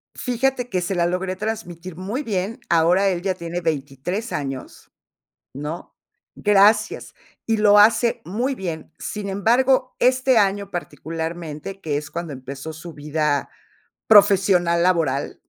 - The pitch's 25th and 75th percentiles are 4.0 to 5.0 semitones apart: Yes, average, 4.5 semitones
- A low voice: No, medium, 185 Hz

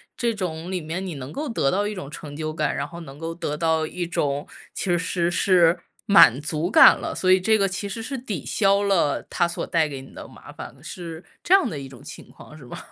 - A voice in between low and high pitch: Yes, medium, 170 Hz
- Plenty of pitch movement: No, average, 4.1 semitones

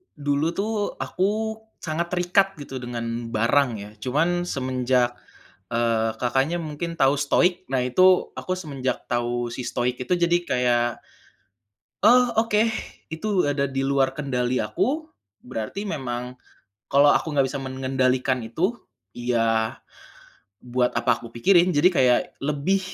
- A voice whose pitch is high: No, low, 135 Hz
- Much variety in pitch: Yes, wide, 5.9 semitones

